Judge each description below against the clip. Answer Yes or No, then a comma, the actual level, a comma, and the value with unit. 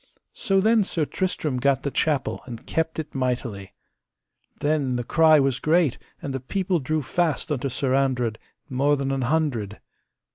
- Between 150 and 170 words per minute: Yes, average, 160 wpm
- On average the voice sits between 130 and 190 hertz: Yes, medium, 140 Hz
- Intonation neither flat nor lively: Yes, average, 3.8 semitones